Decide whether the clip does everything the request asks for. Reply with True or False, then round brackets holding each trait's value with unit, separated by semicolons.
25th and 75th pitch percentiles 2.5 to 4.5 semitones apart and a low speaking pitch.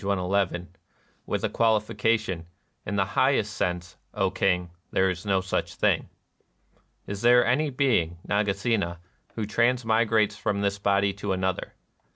True (2.9 semitones; 100 Hz)